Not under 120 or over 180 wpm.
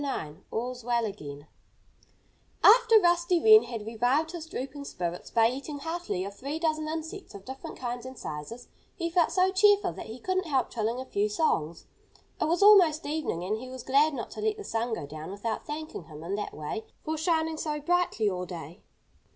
No: average, 195 wpm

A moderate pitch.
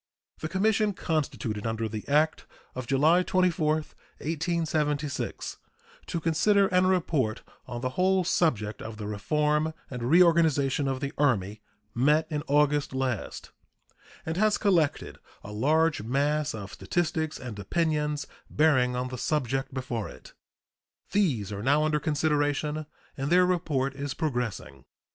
Yes: medium, 150 Hz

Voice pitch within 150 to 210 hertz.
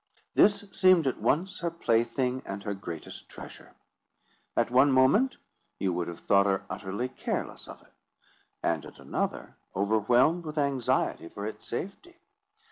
No: low, 125 Hz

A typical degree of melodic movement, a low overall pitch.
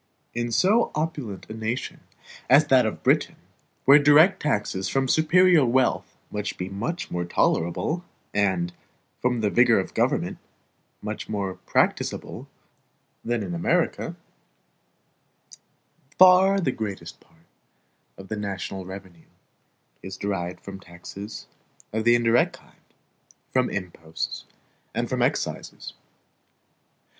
No: wide, 6.0 semitones; low, 110 Hz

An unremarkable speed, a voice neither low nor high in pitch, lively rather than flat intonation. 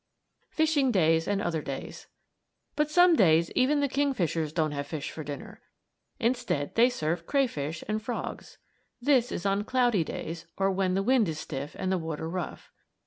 No: average, 170 wpm; high, 195 Hz; wide, 7.6 semitones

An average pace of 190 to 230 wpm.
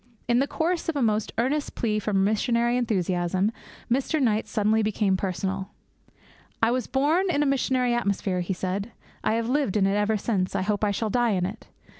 Yes: average, 195 wpm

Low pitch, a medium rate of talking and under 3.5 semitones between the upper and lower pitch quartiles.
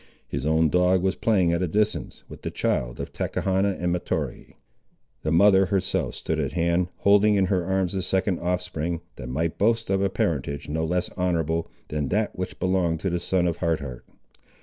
Yes: very low, 90 Hz; average, 195 wpm; average, 2.8 semitones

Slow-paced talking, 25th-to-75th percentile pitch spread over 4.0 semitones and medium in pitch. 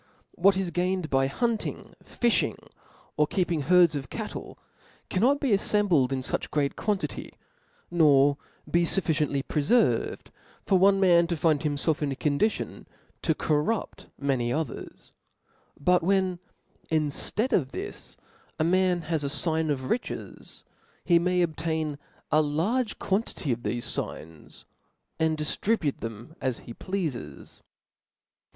Yes: slow, 130 wpm; average, 4.7 semitones; medium, 160 Hz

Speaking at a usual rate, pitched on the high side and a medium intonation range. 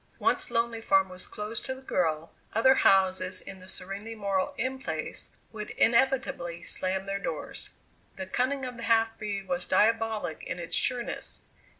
Yes: average, 165 wpm; high, 205 Hz; average, 3.8 semitones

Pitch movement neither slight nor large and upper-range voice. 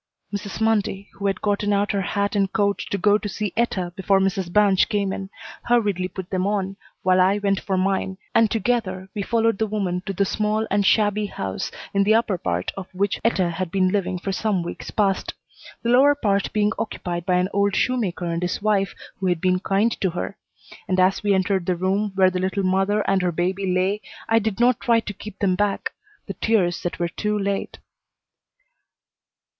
No: narrow, 2.1 semitones; high, 195 Hz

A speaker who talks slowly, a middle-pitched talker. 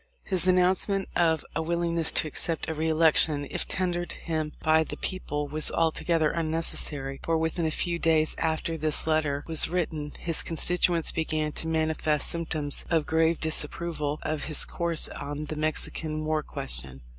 No: average, 160 wpm; medium, 160 Hz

